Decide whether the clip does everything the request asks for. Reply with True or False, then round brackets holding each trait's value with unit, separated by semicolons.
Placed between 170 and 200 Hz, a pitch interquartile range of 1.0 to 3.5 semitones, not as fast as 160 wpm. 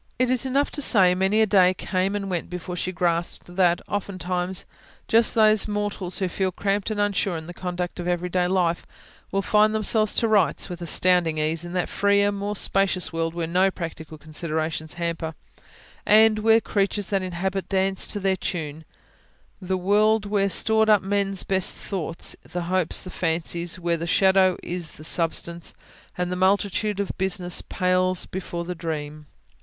False (185 Hz; 2.7 semitones; 175 wpm)